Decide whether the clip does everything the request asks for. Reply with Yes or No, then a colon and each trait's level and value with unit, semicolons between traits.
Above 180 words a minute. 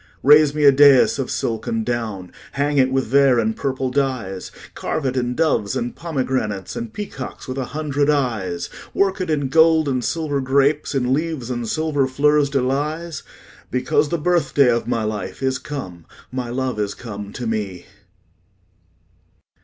No: average, 175 wpm